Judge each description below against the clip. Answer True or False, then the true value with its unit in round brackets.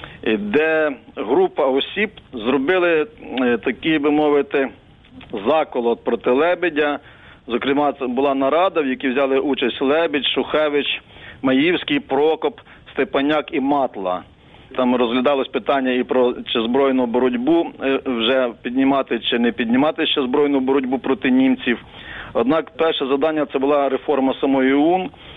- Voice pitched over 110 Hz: True (140 Hz)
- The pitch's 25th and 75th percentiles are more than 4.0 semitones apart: False (3.3 semitones)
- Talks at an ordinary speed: True (120 wpm)